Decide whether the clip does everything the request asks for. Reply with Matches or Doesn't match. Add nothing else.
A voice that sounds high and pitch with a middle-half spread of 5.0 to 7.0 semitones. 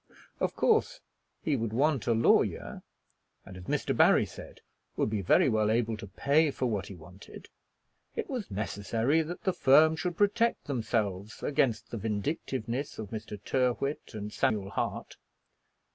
Doesn't match